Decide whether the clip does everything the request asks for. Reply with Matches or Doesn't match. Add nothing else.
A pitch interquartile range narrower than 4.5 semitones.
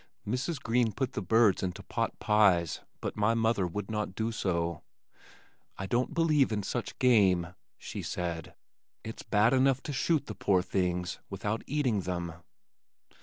Doesn't match